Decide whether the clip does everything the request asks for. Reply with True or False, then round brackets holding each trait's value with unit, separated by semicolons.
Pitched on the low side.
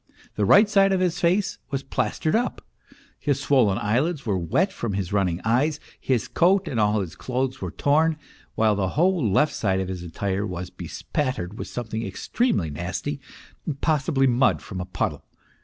True (125 Hz)